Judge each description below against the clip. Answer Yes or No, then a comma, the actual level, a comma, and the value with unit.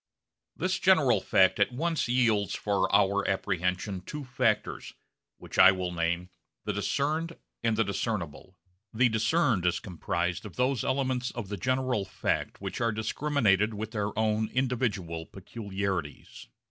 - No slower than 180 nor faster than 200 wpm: No, average, 140 wpm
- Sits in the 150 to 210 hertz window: No, low, 105 Hz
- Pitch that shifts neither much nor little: Yes, average, 4.8 semitones